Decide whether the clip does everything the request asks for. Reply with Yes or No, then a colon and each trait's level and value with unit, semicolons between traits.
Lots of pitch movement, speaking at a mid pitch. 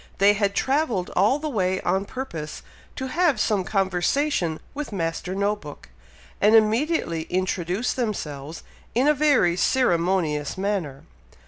No: wide, 6.5 semitones; high, 200 Hz